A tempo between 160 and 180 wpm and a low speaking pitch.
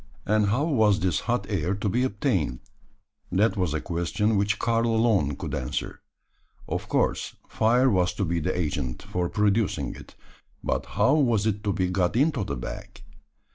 Yes: average, 175 wpm; low, 100 Hz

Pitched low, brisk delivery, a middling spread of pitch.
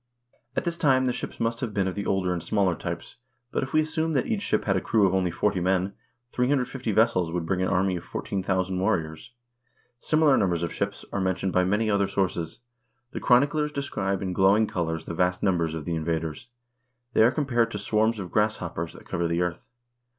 Yes: very low, 95 Hz; fast, 210 wpm; average, 4.8 semitones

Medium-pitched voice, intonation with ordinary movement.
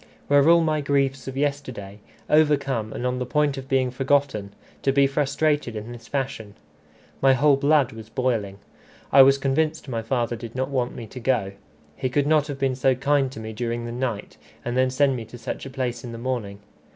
No: low, 130 Hz; average, 3.0 semitones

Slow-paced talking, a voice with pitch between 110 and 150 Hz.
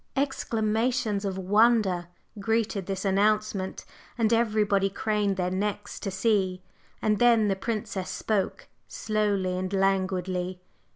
No: slow, 115 wpm; high, 200 Hz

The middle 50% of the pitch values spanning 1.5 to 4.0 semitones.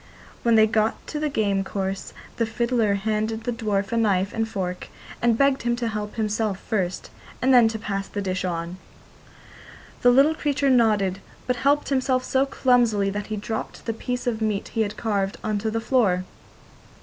Yes: average, 3.3 semitones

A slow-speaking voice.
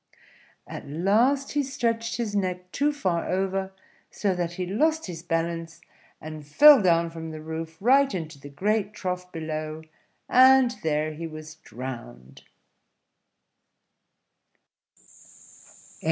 Yes: slow, 120 wpm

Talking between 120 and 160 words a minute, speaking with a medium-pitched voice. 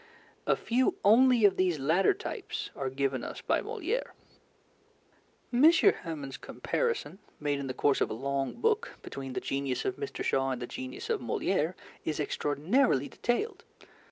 Yes: average, 155 wpm; medium, 150 Hz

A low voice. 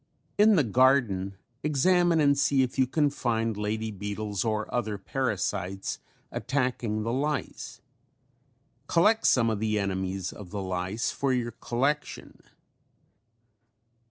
Yes: low, 115 Hz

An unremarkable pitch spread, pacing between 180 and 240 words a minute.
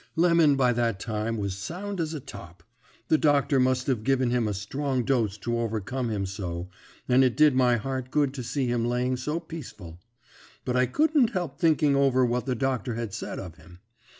Yes: average, 4.0 semitones; average, 200 wpm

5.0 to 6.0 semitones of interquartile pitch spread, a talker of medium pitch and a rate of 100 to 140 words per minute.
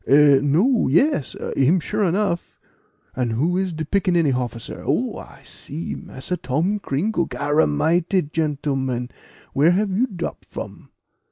Yes: average, 5.3 semitones; medium, 160 Hz; slow, 135 wpm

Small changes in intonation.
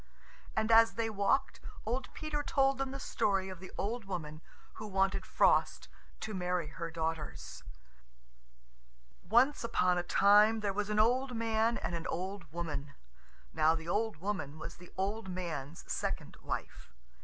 No: average, 4.8 semitones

